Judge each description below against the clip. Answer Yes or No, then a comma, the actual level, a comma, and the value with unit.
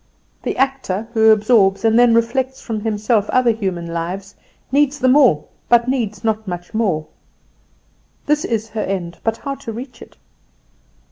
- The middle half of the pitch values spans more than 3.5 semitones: Yes, average, 4.1 semitones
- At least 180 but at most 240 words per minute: No, average, 155 wpm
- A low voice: No, high, 225 Hz